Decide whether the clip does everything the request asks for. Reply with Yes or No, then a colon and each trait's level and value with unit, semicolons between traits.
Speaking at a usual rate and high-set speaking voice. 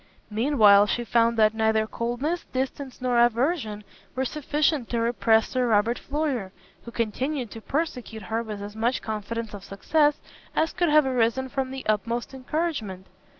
Yes: average, 160 wpm; high, 235 Hz